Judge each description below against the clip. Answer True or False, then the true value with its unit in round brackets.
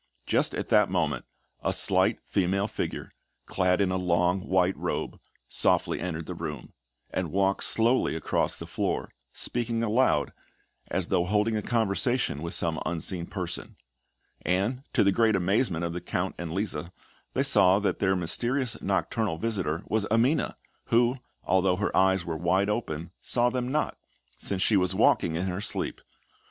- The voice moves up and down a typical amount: True (3.9 semitones)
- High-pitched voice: False (95 Hz)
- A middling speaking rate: True (160 wpm)